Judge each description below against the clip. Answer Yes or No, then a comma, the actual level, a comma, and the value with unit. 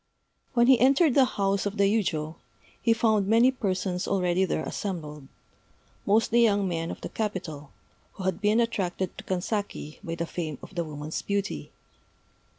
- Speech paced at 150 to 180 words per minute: Yes, average, 160 wpm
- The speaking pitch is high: Yes, high, 195 Hz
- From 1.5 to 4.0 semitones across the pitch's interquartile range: No, average, 4.4 semitones